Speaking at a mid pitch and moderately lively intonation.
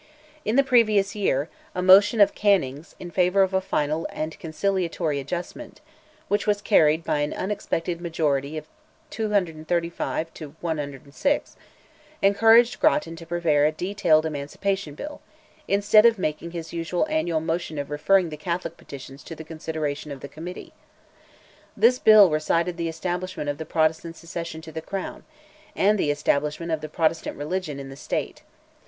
Yes: medium, 165 Hz; average, 4.1 semitones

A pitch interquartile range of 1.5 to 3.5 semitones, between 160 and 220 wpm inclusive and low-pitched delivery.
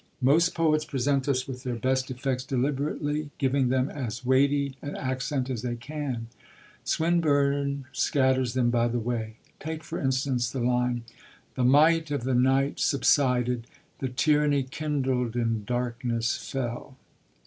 No: narrow, 2.5 semitones; average, 140 wpm; low, 130 Hz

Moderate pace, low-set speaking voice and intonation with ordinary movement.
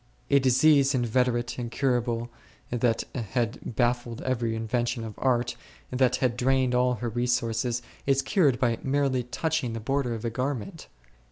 No: average, 145 wpm; low, 125 Hz; narrow, 1.9 semitones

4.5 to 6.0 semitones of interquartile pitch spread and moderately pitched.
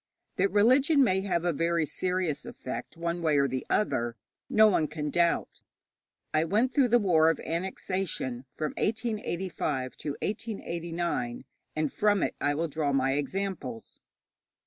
Yes: average, 5.2 semitones; medium, 170 Hz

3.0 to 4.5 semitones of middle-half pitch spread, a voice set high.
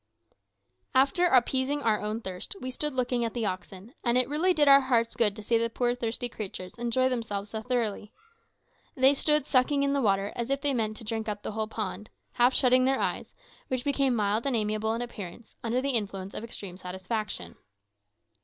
Yes: average, 3.6 semitones; high, 235 Hz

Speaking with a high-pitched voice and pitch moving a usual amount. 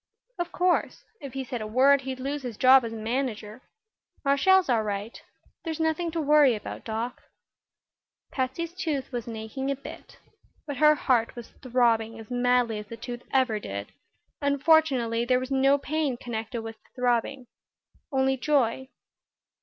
Yes: very high, 255 Hz; average, 3.5 semitones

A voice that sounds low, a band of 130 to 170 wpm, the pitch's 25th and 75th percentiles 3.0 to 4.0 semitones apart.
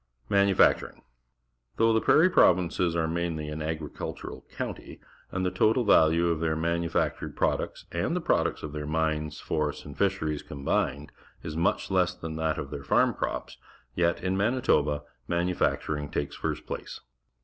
Yes: very low, 80 Hz; average, 155 wpm; average, 3.3 semitones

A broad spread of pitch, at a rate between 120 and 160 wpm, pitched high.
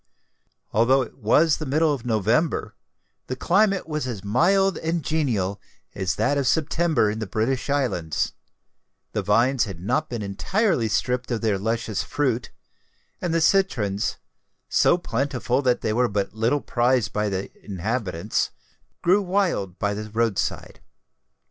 No: wide, 6.4 semitones; average, 150 wpm; low, 120 Hz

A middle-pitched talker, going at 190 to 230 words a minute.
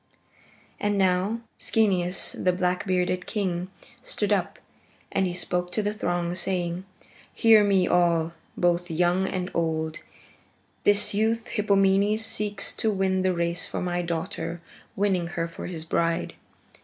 No: medium, 180 Hz; average, 140 wpm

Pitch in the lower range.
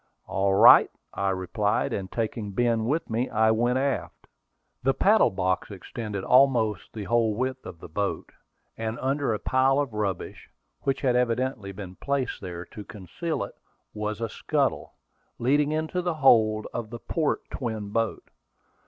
Yes: low, 115 Hz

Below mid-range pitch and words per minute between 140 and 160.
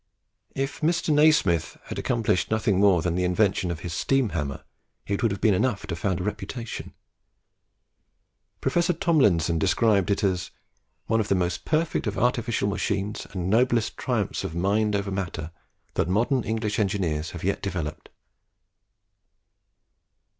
Yes: low, 100 Hz; average, 145 wpm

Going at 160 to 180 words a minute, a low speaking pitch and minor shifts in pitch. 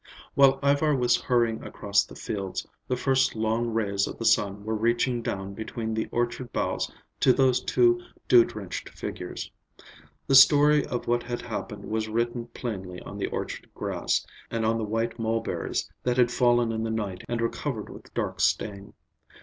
Yes: average, 175 wpm; low, 115 Hz; narrow, 2.2 semitones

